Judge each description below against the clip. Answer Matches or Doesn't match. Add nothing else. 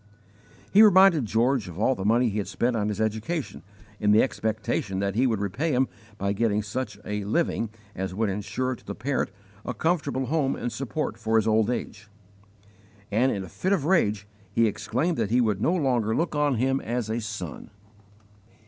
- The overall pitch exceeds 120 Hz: Doesn't match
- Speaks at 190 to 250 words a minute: Matches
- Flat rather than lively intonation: Doesn't match